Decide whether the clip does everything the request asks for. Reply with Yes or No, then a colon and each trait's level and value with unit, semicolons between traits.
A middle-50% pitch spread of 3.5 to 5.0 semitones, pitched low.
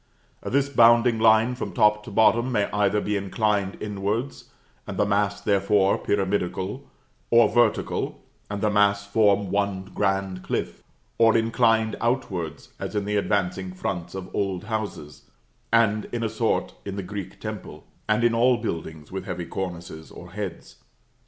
No: average, 2.7 semitones; low, 105 Hz